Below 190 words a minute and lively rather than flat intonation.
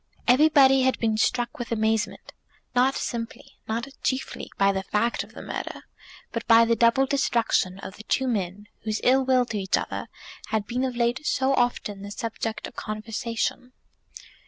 No: average, 170 wpm; average, 2.9 semitones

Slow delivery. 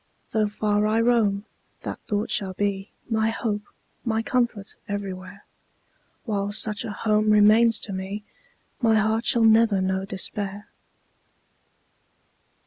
Yes: slow, 125 wpm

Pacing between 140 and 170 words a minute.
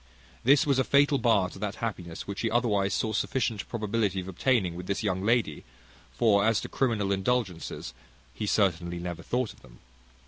No: average, 180 wpm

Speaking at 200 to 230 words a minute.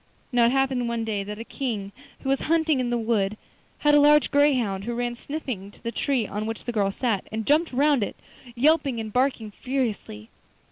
Yes: fast, 205 wpm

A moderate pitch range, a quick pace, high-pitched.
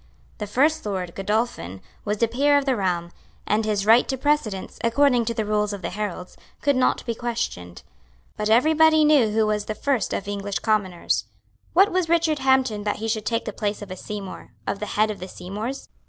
Yes: average, 4.5 semitones; fast, 210 wpm; high, 215 Hz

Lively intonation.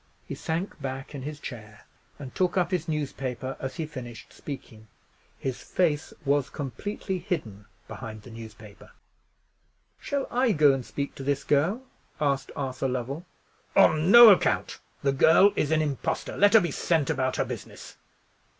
No: average, 4.5 semitones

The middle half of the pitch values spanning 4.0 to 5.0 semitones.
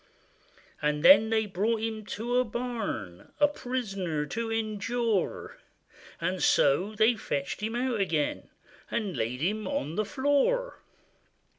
Yes: average, 4.6 semitones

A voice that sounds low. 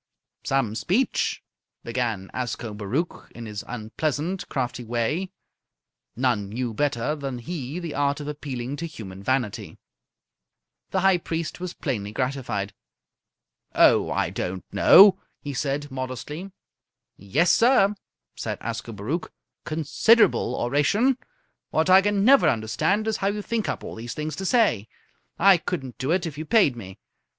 No: medium, 145 Hz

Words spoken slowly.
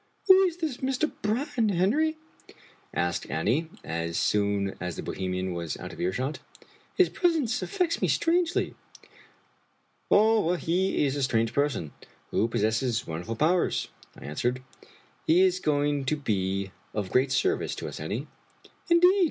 No: average, 155 wpm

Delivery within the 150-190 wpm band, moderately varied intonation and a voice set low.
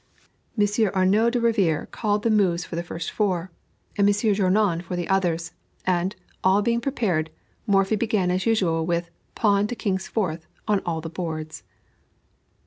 No: average, 160 wpm; average, 3.5 semitones; high, 190 Hz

